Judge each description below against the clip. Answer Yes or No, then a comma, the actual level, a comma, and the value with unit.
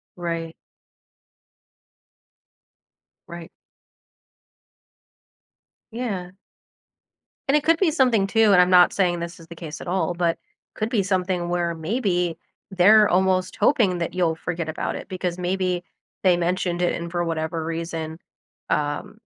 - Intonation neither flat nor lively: No, narrow, 2.2 semitones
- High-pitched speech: No, medium, 180 Hz